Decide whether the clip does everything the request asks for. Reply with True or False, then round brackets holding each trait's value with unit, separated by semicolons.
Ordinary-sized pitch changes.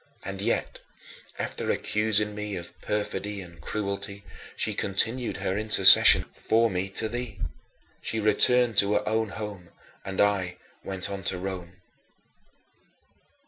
False (2.1 semitones)